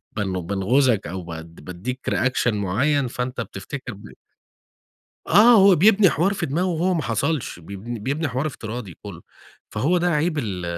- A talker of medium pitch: No, low, 125 Hz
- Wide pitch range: Yes, wide, 7.8 semitones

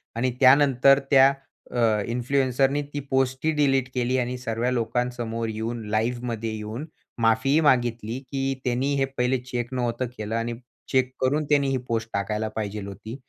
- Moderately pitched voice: No, low, 125 Hz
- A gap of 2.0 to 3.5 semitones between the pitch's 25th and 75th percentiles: Yes, average, 2.8 semitones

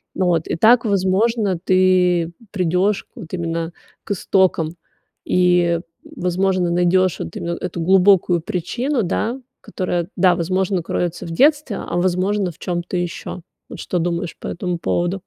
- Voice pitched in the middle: Yes, medium, 180 Hz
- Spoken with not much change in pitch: Yes, narrow, 1.9 semitones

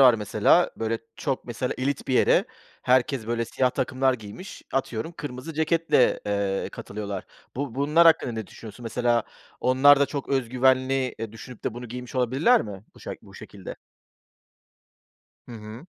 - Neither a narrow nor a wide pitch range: Yes, average, 3.2 semitones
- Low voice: Yes, low, 125 Hz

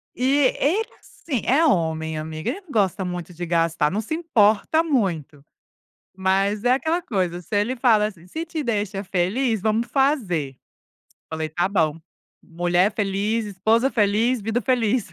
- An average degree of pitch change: No, wide, 6.3 semitones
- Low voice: No, high, 205 Hz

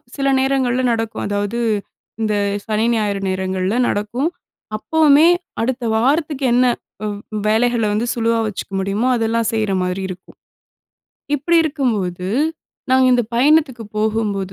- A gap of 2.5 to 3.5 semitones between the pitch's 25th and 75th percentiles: No, average, 4.1 semitones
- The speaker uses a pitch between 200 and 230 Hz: Yes, high, 225 Hz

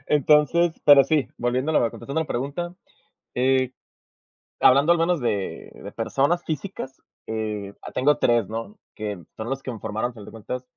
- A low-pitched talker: Yes, low, 130 Hz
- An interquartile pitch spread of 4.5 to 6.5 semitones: Yes, average, 4.8 semitones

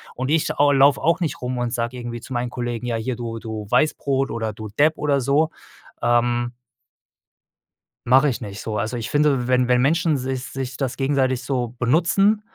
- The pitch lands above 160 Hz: No, low, 125 Hz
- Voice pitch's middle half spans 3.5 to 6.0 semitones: No, average, 2.9 semitones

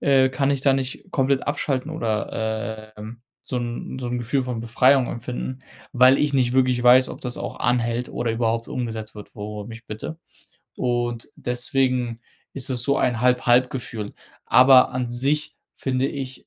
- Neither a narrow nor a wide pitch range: No, narrow, 2.1 semitones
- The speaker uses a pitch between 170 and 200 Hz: No, low, 125 Hz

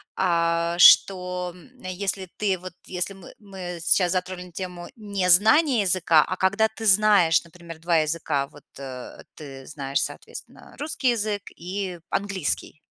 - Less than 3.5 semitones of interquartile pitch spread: Yes, average, 2.9 semitones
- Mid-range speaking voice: Yes, medium, 180 Hz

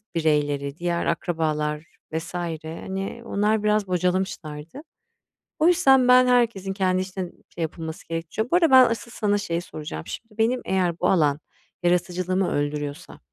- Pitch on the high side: No, medium, 180 Hz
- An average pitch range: Yes, average, 4.8 semitones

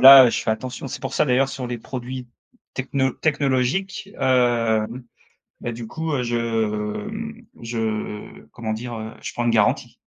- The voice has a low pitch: Yes, low, 125 Hz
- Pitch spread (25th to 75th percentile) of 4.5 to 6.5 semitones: No, average, 2.9 semitones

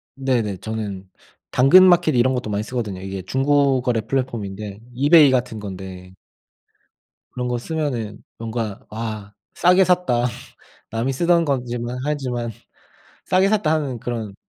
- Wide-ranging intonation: No, average, 4.7 semitones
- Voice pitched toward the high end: No, low, 120 Hz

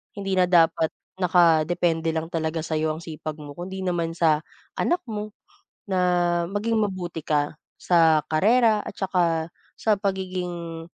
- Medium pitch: Yes, medium, 170 Hz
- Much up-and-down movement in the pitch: No, average, 2.9 semitones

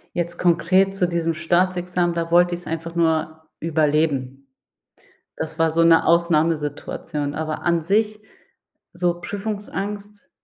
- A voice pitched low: No, medium, 170 Hz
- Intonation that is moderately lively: No, narrow, 2.0 semitones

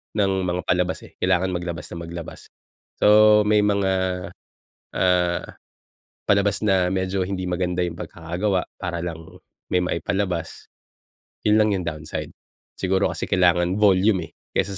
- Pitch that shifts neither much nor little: No, narrow, 1.9 semitones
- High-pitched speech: No, very low, 90 Hz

